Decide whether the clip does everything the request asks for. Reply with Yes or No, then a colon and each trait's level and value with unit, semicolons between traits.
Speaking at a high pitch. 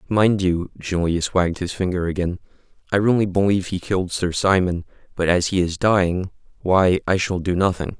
No: very low, 90 Hz